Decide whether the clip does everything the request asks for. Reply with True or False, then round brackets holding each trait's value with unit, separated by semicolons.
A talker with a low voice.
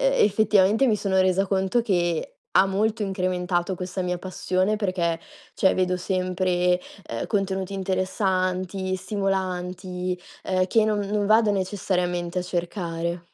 False (185 Hz)